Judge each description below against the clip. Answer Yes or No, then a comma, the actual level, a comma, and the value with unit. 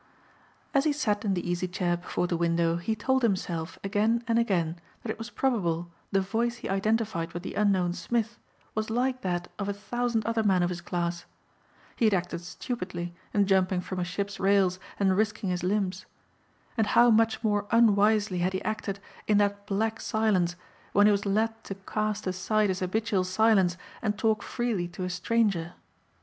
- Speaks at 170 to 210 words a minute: Yes, average, 185 wpm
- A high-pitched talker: Yes, high, 200 Hz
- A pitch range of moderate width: Yes, average, 3.4 semitones